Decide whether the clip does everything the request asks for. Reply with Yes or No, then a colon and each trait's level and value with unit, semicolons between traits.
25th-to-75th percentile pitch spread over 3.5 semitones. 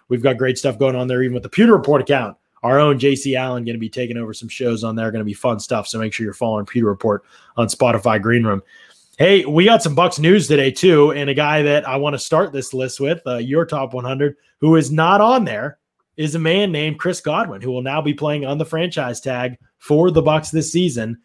Yes: average, 4.1 semitones